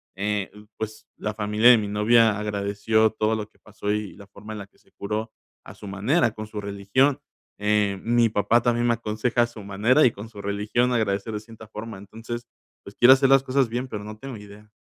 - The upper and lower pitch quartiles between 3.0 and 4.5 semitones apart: No, narrow, 2.4 semitones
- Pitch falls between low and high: No, low, 110 Hz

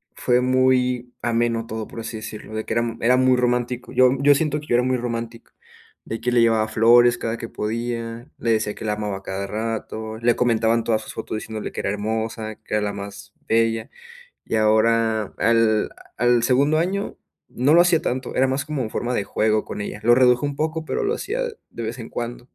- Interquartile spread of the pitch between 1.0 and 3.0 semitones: Yes, narrow, 2.4 semitones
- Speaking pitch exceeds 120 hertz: No, low, 115 Hz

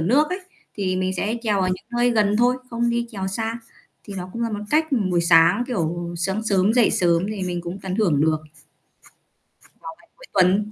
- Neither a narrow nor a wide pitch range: Yes, average, 4.5 semitones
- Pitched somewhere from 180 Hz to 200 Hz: Yes, high, 195 Hz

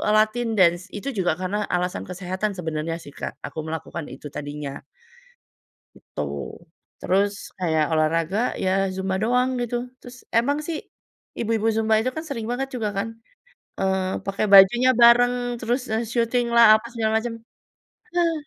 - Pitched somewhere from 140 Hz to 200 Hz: No, high, 215 Hz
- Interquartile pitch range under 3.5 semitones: No, average, 5.0 semitones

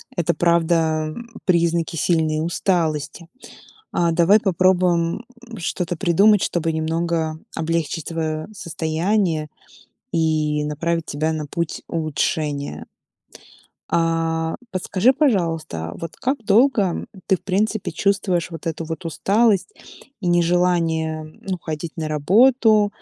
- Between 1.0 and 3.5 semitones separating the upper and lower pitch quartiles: Yes, average, 2.8 semitones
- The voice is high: No, medium, 170 Hz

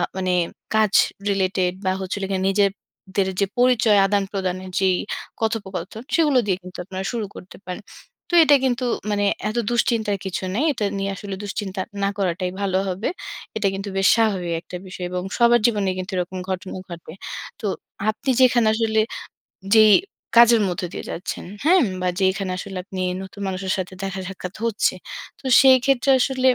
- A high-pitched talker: Yes, high, 195 Hz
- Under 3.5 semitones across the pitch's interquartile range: Yes, average, 3.0 semitones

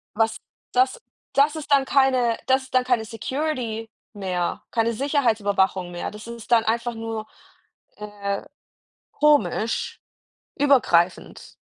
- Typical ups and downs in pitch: Yes, average, 3.7 semitones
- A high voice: Yes, high, 230 Hz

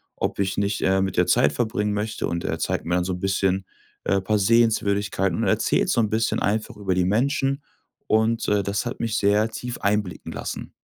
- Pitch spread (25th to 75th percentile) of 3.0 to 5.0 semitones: No, narrow, 2.5 semitones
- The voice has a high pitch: No, low, 105 Hz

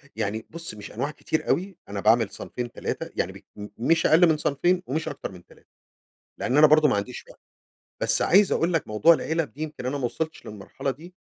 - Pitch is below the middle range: No, medium, 150 Hz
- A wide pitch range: Yes, wide, 6.2 semitones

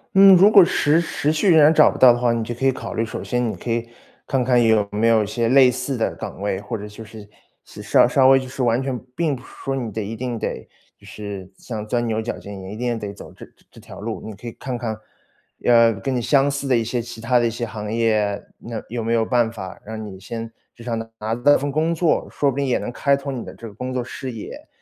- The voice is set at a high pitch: No, low, 120 Hz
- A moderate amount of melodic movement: Yes, average, 3.0 semitones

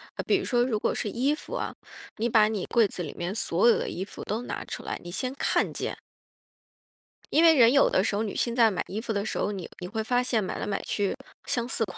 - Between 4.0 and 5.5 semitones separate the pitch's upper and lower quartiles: No, average, 3.5 semitones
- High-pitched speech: Yes, high, 220 Hz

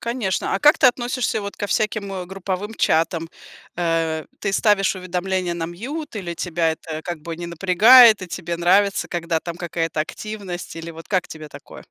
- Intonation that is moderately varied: Yes, average, 3.5 semitones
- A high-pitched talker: No, medium, 180 Hz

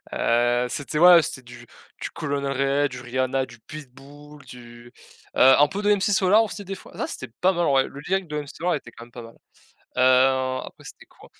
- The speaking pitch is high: No, low, 135 Hz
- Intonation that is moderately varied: Yes, average, 3.5 semitones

